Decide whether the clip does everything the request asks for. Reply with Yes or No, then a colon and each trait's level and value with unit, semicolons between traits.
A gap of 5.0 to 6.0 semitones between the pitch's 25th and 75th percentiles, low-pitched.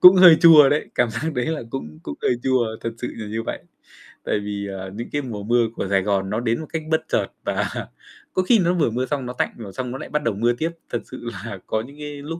Yes: wide, 5.4 semitones; low, 125 Hz